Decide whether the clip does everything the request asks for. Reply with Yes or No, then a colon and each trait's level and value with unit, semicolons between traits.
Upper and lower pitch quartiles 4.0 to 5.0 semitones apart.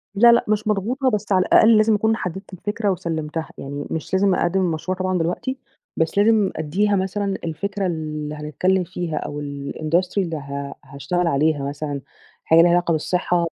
Yes: average, 4.4 semitones